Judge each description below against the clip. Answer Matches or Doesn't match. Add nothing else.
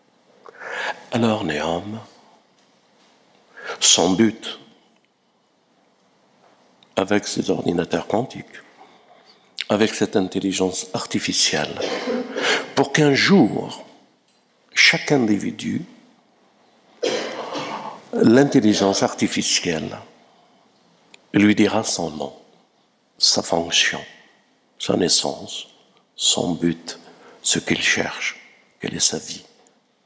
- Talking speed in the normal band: Doesn't match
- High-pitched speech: Doesn't match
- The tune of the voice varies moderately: Matches